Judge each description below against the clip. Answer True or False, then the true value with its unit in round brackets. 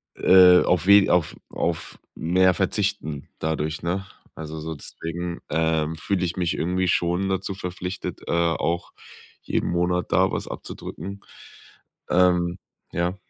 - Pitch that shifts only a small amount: True (2.0 semitones)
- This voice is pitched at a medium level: False (90 Hz)